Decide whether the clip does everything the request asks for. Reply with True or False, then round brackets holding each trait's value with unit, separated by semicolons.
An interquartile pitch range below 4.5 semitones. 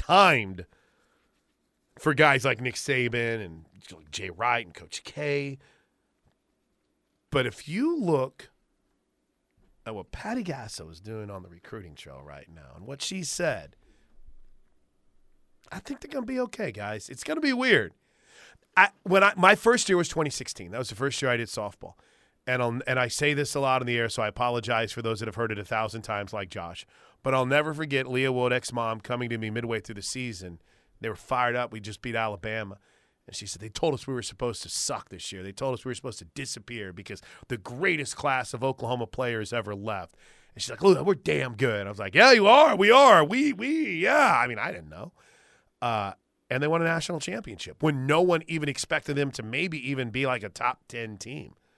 False (5.3 semitones)